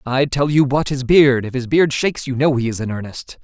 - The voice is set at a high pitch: No, low, 135 Hz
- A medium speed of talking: No, fast, 260 wpm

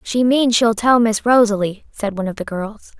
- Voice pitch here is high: Yes, high, 220 Hz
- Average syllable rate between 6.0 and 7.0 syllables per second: No, 5.3 syllables/s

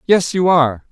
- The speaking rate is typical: Yes, average, 195 wpm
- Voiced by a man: Yes, male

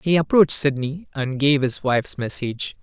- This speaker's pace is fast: No, average, 170 wpm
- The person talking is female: No, male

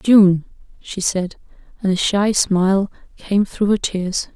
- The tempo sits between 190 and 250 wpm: No, average, 150 wpm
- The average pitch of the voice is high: Yes, high, 195 Hz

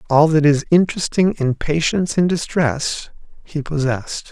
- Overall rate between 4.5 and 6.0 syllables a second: Yes, 4.8 syllables/s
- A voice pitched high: No, medium, 155 Hz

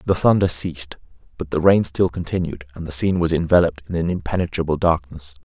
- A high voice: No, very low, 80 Hz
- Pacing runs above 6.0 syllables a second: Yes, 6.4 syllables/s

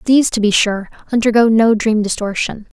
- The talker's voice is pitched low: No, high, 220 Hz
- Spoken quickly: No, average, 170 wpm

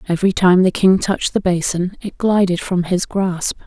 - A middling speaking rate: Yes, average, 195 wpm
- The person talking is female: Yes, female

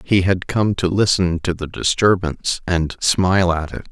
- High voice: No, very low, 90 Hz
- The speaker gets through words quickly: No, average, 185 wpm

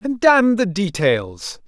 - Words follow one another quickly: No, average, 145 wpm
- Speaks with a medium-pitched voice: No, high, 195 Hz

